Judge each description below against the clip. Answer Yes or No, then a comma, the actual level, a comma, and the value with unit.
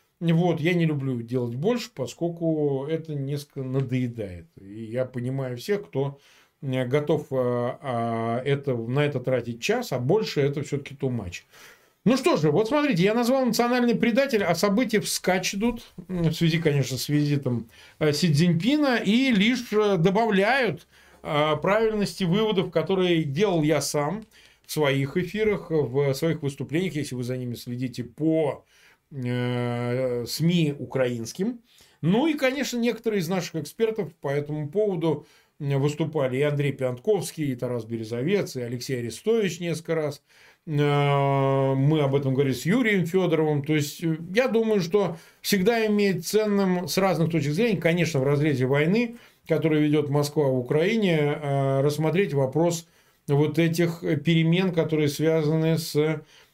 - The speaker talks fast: No, average, 135 wpm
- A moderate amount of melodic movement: No, wide, 5.8 semitones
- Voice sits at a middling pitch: Yes, medium, 155 Hz